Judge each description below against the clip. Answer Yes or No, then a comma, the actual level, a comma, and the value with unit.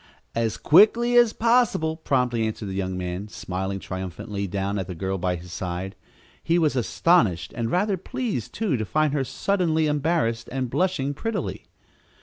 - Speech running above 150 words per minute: Yes, average, 160 wpm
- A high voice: No, low, 125 Hz